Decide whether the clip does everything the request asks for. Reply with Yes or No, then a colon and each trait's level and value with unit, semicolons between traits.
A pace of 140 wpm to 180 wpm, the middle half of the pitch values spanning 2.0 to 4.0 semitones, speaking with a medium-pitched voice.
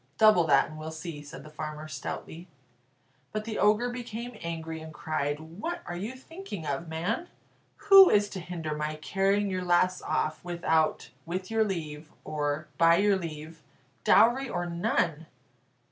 No: average, 160 wpm; average, 5.0 semitones; medium, 170 Hz